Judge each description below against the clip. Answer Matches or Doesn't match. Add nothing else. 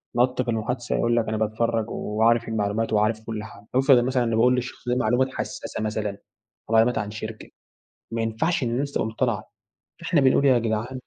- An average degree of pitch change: Doesn't match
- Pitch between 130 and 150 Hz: Doesn't match